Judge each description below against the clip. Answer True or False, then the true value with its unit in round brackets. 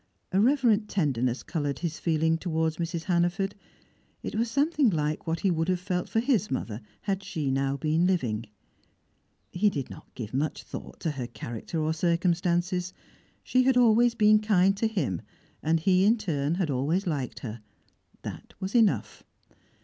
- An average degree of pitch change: True (5.0 semitones)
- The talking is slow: False (165 wpm)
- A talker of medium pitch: True (175 Hz)